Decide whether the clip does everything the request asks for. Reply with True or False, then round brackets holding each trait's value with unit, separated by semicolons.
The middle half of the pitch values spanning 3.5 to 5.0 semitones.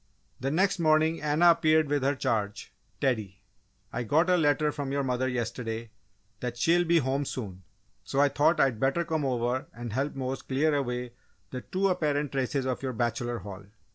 True (4.0 semitones)